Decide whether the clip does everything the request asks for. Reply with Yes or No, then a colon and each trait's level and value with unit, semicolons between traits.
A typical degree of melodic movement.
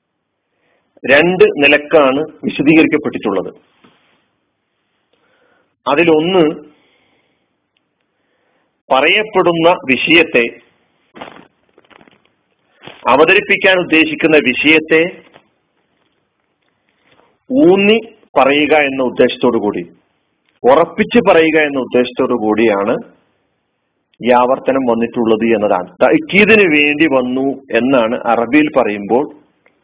No: wide, 6.5 semitones